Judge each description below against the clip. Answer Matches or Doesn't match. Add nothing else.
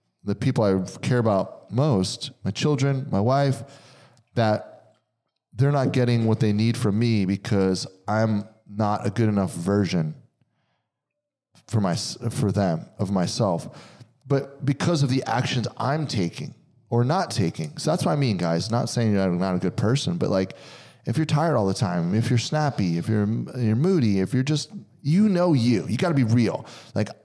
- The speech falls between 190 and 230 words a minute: Doesn't match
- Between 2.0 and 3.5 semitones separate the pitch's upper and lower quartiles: Doesn't match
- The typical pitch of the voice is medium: Doesn't match